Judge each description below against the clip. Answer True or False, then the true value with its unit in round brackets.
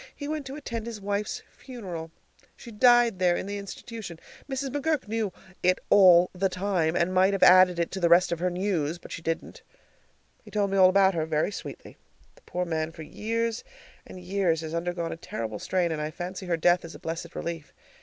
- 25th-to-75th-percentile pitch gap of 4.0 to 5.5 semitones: False (3.5 semitones)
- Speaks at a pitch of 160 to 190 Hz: True (185 Hz)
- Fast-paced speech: True (210 wpm)